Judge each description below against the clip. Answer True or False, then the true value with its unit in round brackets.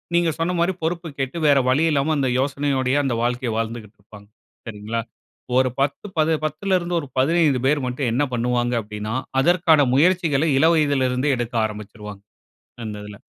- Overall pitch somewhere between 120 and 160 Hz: True (135 Hz)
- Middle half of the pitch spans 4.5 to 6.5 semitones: True (5.1 semitones)